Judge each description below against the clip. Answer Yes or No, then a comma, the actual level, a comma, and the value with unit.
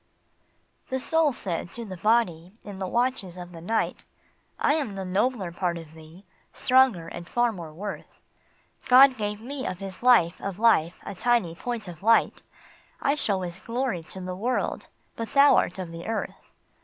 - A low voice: No, high, 200 Hz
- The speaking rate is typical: Yes, average, 180 wpm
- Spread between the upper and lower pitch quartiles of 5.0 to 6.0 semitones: Yes, wide, 5.5 semitones